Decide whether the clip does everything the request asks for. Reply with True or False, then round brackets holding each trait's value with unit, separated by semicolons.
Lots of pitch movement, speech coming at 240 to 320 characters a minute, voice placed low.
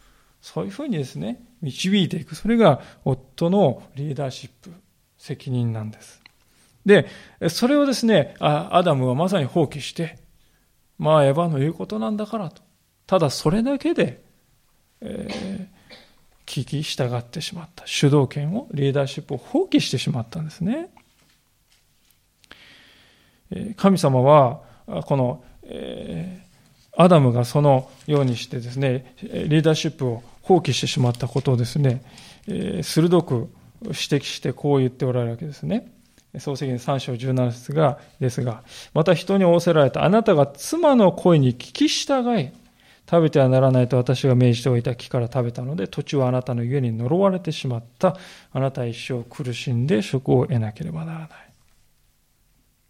False (5.9 semitones; 300 characters per minute; 145 Hz)